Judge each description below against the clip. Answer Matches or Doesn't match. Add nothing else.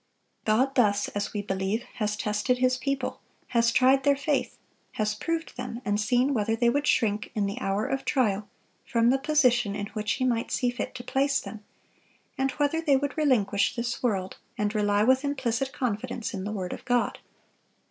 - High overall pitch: Matches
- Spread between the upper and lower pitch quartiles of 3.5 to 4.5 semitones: Matches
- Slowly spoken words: Doesn't match